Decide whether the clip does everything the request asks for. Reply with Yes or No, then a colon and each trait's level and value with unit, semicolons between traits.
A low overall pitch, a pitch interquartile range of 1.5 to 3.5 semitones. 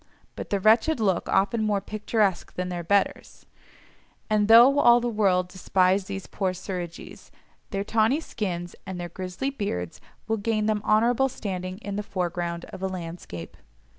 No: high, 200 Hz; average, 3.1 semitones